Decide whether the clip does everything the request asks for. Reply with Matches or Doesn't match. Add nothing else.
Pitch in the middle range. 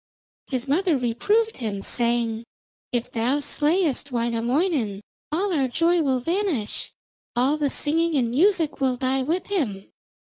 Doesn't match